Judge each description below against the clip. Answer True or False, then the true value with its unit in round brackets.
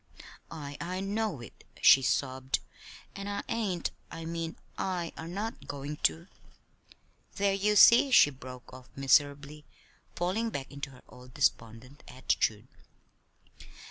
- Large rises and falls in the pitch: True (6.4 semitones)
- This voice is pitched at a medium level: True (150 Hz)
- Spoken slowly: True (130 wpm)